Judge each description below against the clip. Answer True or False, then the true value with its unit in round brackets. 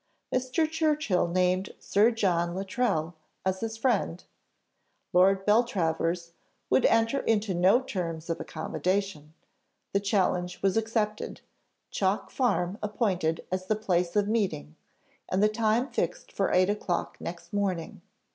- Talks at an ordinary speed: False (130 wpm)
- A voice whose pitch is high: True (195 Hz)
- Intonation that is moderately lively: True (3.9 semitones)